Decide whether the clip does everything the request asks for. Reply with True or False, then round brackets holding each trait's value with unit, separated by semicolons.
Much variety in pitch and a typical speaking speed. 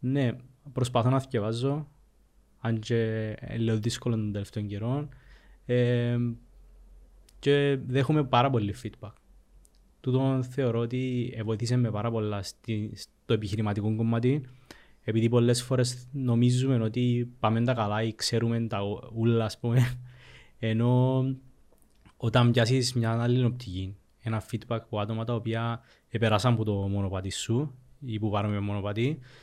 False (2.8 semitones; 130 wpm)